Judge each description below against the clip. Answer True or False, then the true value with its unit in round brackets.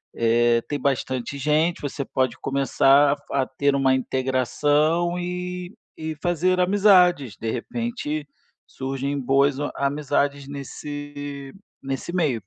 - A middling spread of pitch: True (3.0 semitones)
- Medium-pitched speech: True (145 Hz)